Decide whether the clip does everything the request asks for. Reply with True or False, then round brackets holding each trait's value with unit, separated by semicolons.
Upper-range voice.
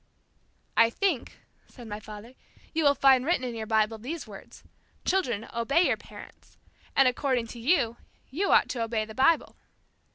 True (245 Hz)